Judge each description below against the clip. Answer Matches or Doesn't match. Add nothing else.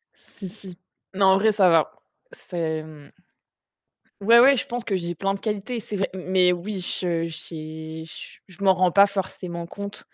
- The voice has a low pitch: Doesn't match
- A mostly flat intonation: Doesn't match